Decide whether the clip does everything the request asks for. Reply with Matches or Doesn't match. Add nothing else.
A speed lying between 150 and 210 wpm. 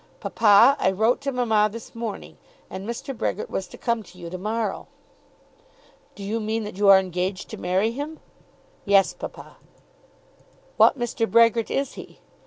Matches